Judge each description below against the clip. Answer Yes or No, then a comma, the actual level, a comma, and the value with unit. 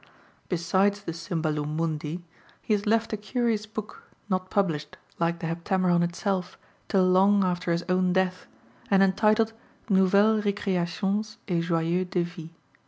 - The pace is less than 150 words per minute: Yes, slow, 135 wpm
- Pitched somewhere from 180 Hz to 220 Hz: Yes, medium, 185 Hz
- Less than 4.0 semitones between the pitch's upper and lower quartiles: Yes, average, 3.0 semitones